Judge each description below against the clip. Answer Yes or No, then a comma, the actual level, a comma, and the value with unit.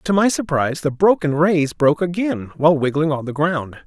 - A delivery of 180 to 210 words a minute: Yes, average, 200 wpm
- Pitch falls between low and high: Yes, medium, 160 Hz